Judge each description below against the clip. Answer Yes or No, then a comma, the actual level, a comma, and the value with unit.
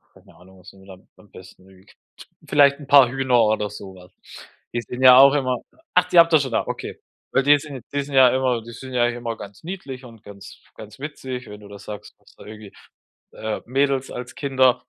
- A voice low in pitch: Yes, low, 125 Hz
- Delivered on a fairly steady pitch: No, average, 4.6 semitones